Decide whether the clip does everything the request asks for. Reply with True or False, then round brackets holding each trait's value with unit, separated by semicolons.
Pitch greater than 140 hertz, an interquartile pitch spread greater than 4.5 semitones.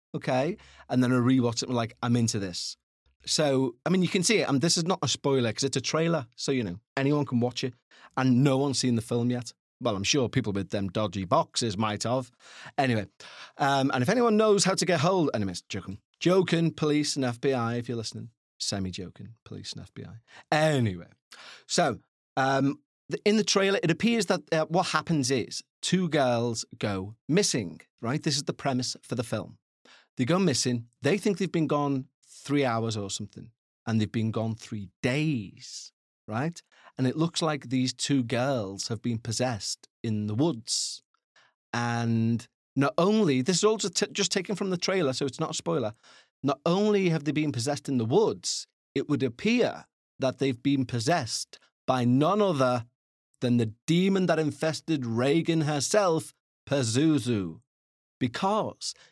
False (135 Hz; 5.4 semitones)